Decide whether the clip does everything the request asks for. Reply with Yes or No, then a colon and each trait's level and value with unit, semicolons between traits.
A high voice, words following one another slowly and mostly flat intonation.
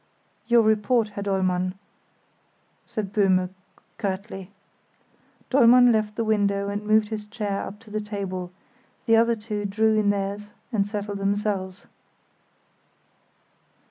Yes: high, 210 Hz; slow, 120 wpm; narrow, 1.6 semitones